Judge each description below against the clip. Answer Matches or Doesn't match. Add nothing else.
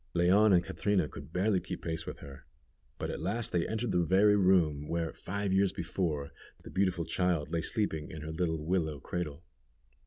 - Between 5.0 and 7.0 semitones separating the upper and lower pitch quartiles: Doesn't match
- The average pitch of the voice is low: Matches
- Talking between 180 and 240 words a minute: Matches